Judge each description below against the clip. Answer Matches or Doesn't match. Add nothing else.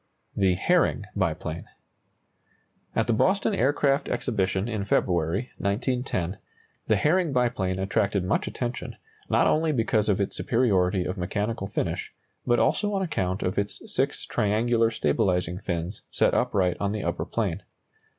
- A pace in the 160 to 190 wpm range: Doesn't match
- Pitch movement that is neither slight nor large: Matches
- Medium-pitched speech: Doesn't match